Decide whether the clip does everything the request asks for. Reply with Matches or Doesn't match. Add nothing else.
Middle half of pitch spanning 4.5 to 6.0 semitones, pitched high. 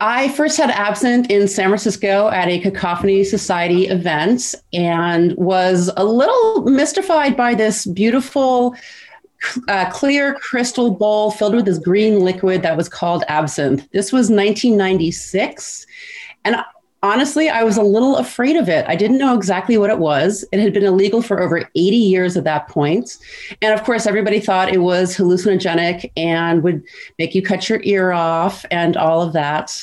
Matches